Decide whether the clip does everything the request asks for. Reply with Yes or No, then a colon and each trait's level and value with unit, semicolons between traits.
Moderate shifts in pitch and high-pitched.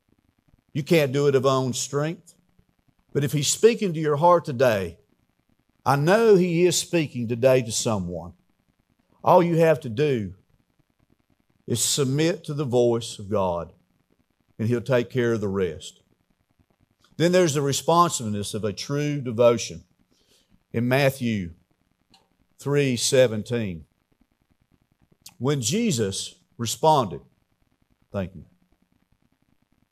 No: average, 4.8 semitones; low, 130 Hz